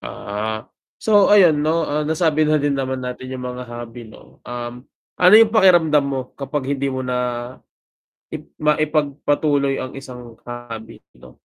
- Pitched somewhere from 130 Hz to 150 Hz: Yes, medium, 140 Hz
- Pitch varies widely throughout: No, average, 3.8 semitones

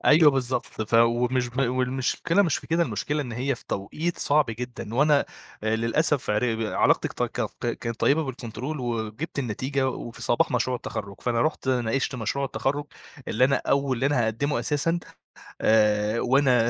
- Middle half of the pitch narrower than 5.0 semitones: Yes, average, 3.4 semitones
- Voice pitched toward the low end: Yes, low, 125 Hz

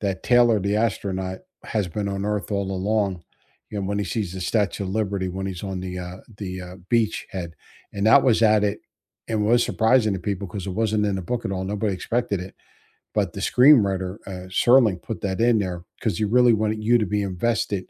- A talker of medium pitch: No, low, 100 Hz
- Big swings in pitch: No, average, 2.7 semitones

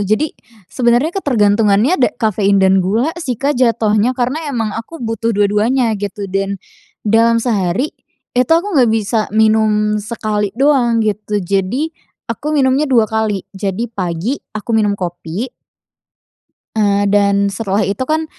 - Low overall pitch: No, high, 220 Hz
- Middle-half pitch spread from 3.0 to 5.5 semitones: Yes, average, 3.5 semitones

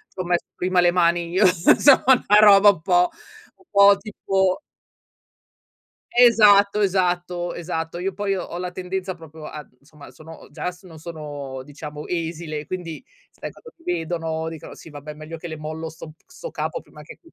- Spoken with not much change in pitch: No, average, 3.1 semitones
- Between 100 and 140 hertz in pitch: No, medium, 175 Hz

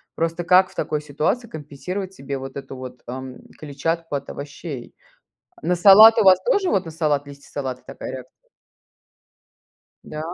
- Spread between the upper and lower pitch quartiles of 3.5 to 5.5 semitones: Yes, average, 4.9 semitones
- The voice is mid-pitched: Yes, medium, 150 Hz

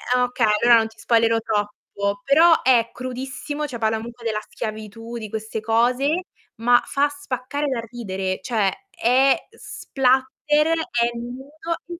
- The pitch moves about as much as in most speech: Yes, average, 3.4 semitones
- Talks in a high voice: Yes, high, 240 Hz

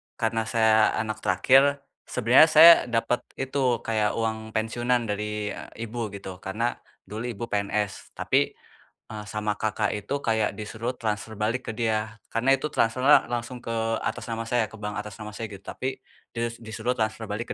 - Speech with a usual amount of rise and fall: No, narrow, 2.2 semitones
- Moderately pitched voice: No, low, 110 Hz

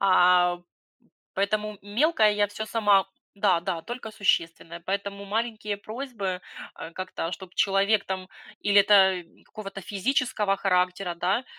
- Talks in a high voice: Yes, high, 200 Hz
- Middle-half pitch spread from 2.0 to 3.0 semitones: Yes, narrow, 2.4 semitones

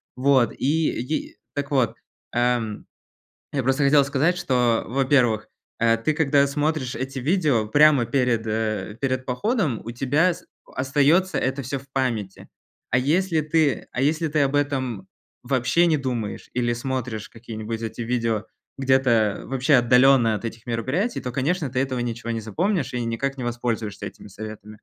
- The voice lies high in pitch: No, low, 130 Hz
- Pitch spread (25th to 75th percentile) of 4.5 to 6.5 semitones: No, average, 3.5 semitones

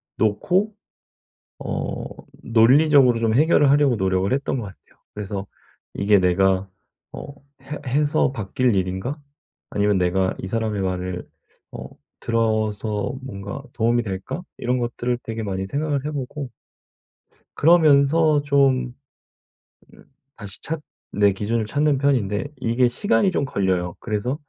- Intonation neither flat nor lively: No, wide, 5.9 semitones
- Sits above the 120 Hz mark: No, low, 115 Hz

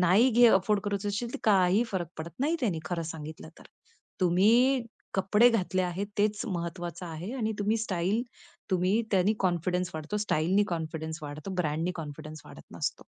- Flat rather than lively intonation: No, average, 3.8 semitones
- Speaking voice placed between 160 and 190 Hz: Yes, medium, 185 Hz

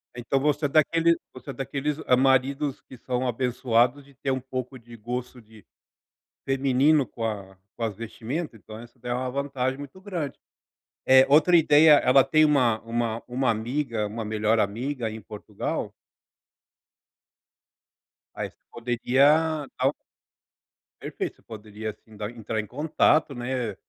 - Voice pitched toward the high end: No, low, 125 Hz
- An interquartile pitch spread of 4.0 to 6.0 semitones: No, average, 3.5 semitones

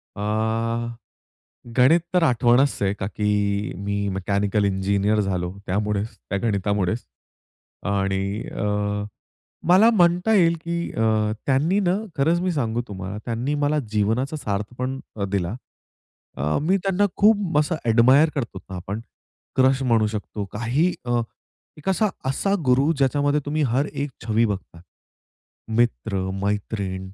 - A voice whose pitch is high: No, low, 115 Hz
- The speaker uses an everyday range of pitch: No, wide, 6.6 semitones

